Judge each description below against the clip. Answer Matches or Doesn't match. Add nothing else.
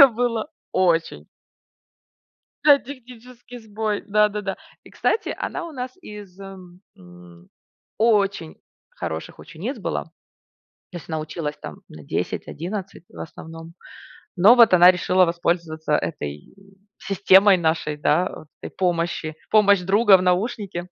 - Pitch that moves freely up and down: Doesn't match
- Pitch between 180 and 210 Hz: Matches